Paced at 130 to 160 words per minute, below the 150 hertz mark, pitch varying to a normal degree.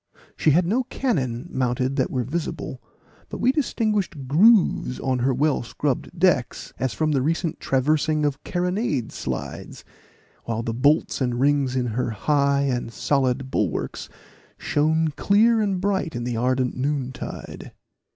Yes: average, 145 wpm; medium, 140 Hz; average, 4.9 semitones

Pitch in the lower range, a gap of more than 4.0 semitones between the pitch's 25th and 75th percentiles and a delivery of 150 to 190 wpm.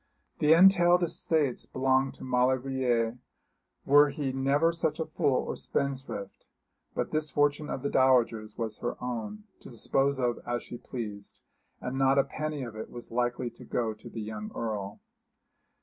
No: low, 130 Hz; average, 3.5 semitones; average, 165 wpm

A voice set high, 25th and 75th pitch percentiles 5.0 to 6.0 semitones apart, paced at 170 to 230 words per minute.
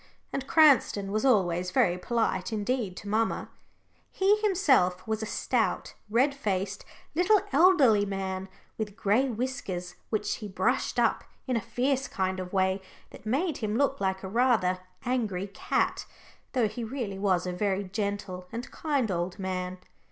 No: high, 210 Hz; average, 5.3 semitones; average, 155 wpm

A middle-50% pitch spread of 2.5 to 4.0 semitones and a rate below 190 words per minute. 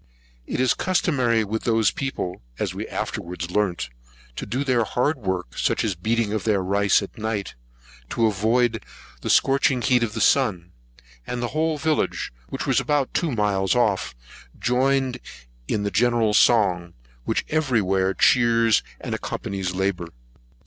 No: average, 4.4 semitones; average, 155 wpm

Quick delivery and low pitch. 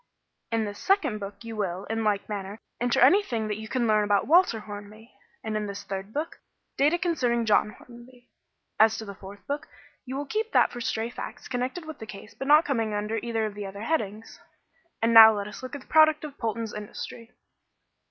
No: fast, 210 wpm; high, 225 Hz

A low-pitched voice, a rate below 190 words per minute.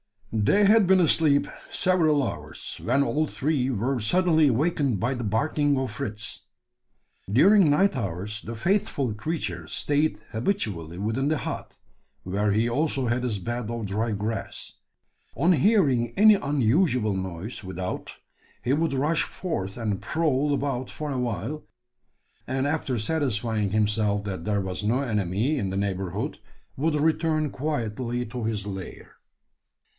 Yes: low, 125 Hz; average, 140 wpm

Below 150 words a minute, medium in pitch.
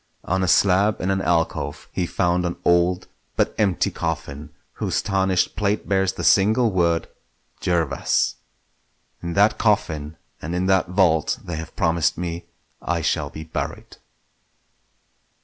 No: average, 140 wpm; very low, 90 Hz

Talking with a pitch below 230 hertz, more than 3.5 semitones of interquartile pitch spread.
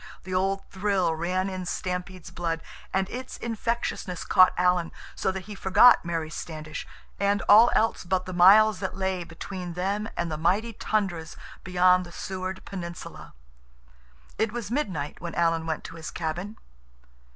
No: medium, 185 Hz; narrow, 2.6 semitones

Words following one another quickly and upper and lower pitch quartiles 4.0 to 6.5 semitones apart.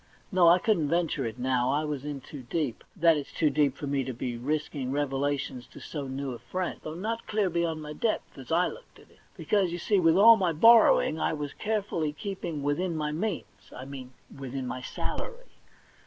Yes: fast, 215 wpm; average, 4.7 semitones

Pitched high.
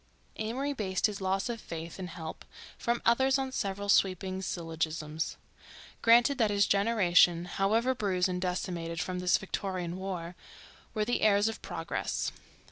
Yes: high, 195 Hz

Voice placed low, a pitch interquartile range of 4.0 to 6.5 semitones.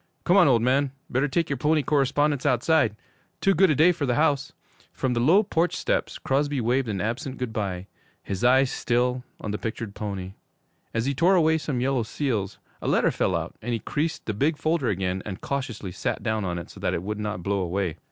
Yes: low, 125 Hz; wide, 5.5 semitones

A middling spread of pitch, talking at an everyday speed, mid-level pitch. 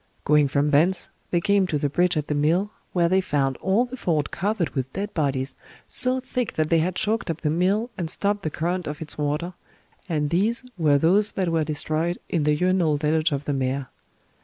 No: average, 4.1 semitones; fast, 210 wpm; medium, 165 Hz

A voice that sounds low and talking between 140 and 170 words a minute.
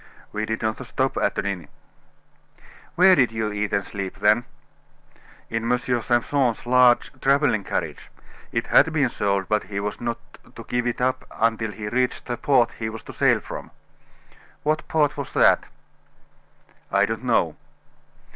Yes: low, 115 Hz; average, 160 wpm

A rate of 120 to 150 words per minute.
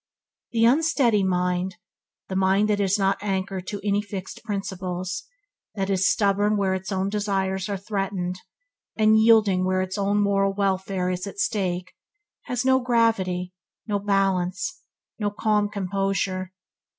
Yes: average, 140 wpm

